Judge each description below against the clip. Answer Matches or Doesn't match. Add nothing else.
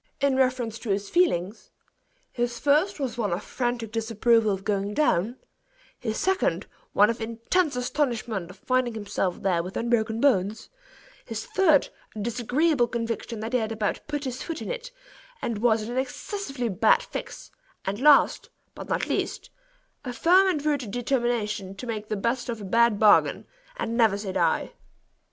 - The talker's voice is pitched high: Matches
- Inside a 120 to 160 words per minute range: Doesn't match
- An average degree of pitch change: Matches